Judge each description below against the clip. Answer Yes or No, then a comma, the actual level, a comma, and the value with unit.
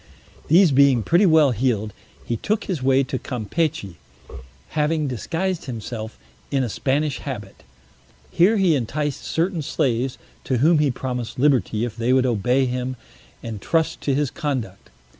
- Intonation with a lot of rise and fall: No, average, 4.3 semitones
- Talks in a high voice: No, low, 135 Hz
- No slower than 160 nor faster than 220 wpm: No, average, 150 wpm